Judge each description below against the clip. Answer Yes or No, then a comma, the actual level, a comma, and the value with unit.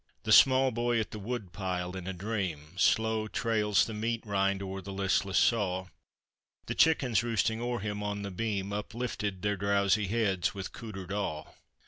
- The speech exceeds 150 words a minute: Yes, average, 165 wpm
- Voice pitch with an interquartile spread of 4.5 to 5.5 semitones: No, average, 2.7 semitones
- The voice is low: Yes, low, 105 Hz